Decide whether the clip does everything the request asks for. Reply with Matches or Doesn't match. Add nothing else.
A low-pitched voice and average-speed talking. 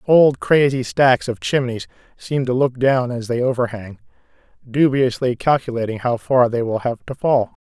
Matches